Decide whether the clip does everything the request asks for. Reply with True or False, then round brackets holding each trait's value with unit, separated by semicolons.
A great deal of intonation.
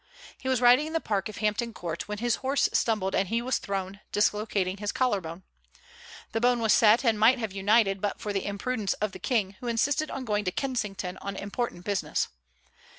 False (3.6 semitones)